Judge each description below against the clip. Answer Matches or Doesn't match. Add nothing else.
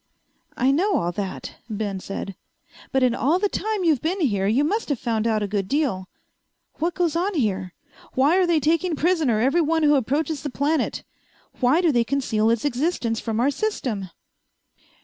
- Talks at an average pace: Matches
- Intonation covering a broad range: Matches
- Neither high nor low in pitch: Doesn't match